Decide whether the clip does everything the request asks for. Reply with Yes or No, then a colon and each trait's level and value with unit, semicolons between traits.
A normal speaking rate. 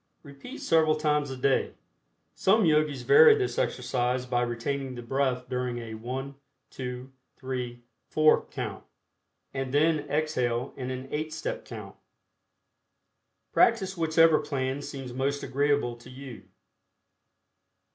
No: slow, 125 wpm